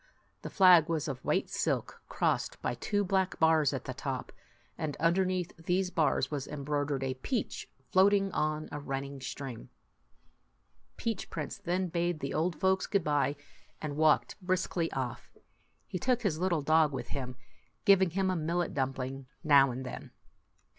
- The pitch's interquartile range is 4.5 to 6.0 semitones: Yes, average, 4.9 semitones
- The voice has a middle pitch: Yes, medium, 155 Hz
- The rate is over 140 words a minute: Yes, average, 160 wpm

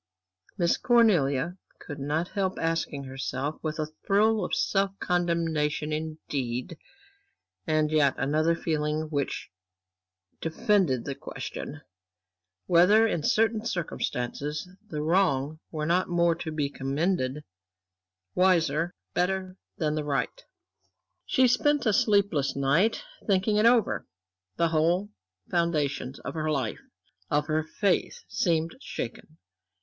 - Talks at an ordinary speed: No, slow, 115 wpm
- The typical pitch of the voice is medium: Yes, medium, 160 Hz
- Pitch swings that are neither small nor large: Yes, average, 4.0 semitones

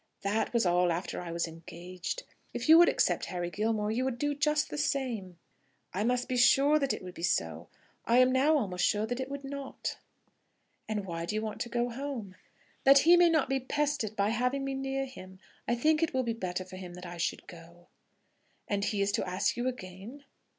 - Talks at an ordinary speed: No, fast, 220 wpm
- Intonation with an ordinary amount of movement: No, wide, 6.6 semitones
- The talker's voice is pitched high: Yes, high, 230 Hz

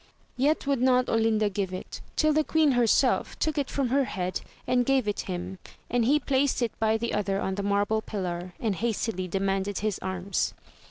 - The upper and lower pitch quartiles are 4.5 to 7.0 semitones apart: Yes, average, 4.8 semitones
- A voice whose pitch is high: Yes, high, 220 Hz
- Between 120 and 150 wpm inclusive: No, average, 195 wpm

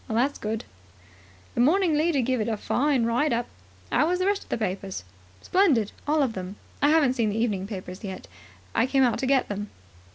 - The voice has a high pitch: Yes, high, 245 Hz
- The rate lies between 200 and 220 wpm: Yes, fast, 205 wpm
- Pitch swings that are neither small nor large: No, wide, 5.7 semitones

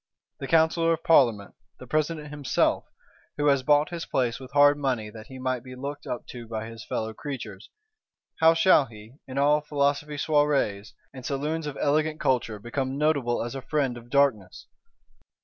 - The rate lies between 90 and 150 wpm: No, average, 175 wpm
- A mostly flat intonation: No, average, 3.7 semitones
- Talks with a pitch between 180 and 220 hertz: No, medium, 140 Hz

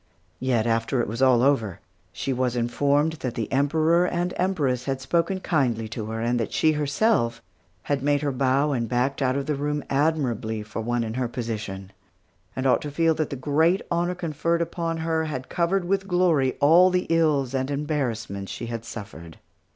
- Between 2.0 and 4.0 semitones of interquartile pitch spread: No, average, 5.1 semitones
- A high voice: No, medium, 140 Hz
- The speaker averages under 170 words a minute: No, average, 190 wpm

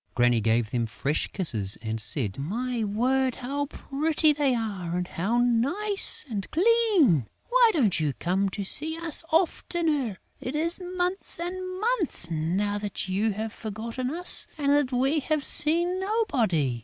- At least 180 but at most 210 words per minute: No, average, 155 wpm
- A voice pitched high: Yes, very high, 250 Hz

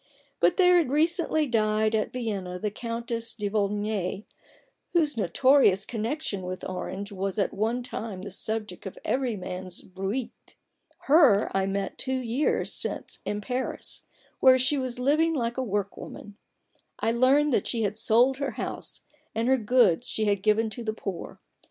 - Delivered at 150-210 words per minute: Yes, average, 165 wpm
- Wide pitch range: No, average, 4.3 semitones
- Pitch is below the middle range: No, high, 225 Hz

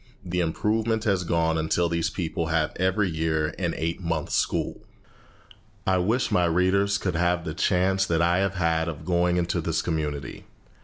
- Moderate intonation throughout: No, narrow, 2.3 semitones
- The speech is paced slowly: No, average, 175 wpm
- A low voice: Yes, very low, 85 Hz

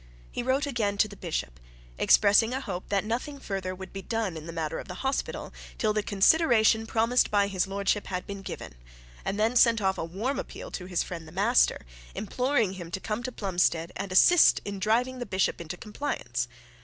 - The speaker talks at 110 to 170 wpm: No, fast, 205 wpm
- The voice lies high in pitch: Yes, high, 200 Hz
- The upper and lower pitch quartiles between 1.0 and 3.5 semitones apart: No, average, 4.0 semitones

